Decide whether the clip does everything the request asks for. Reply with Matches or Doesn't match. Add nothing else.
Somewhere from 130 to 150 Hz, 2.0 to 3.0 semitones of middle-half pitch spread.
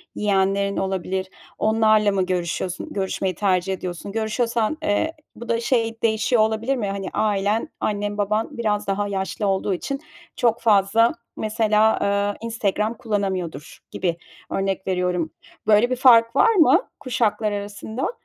Doesn't match